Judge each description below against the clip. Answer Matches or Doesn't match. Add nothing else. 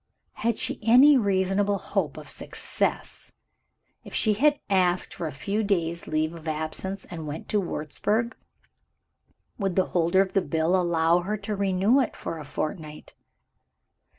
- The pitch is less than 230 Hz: Matches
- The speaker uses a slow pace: Doesn't match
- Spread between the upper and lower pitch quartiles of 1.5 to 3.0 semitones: Doesn't match